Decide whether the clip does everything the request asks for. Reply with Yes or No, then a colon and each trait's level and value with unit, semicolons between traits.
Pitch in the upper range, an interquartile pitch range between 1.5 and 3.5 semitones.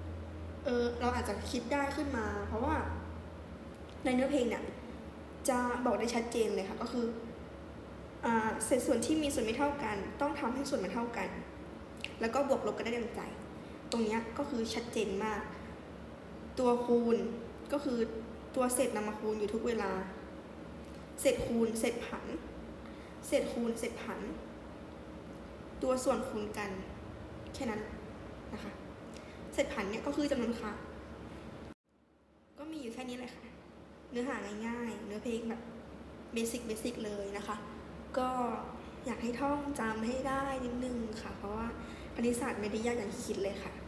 Yes: high, 235 Hz; average, 2.7 semitones